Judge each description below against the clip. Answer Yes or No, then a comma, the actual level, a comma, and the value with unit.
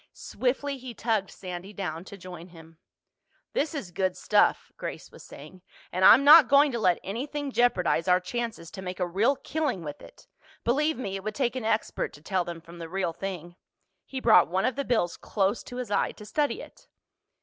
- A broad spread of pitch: Yes, wide, 6.0 semitones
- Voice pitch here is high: Yes, high, 200 Hz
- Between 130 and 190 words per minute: No, fast, 205 wpm